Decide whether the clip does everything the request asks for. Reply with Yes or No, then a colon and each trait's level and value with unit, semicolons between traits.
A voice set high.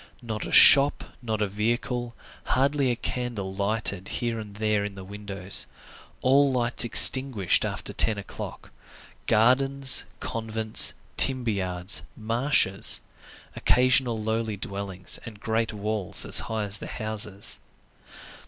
No: low, 110 Hz